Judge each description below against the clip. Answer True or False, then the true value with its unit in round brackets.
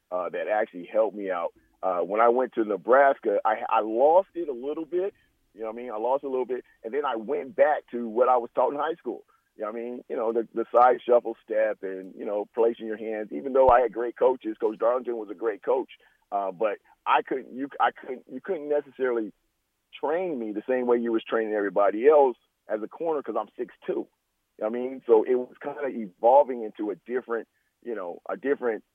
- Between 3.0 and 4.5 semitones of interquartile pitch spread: True (3.9 semitones)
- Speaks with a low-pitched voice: True (120 Hz)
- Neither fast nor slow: False (240 wpm)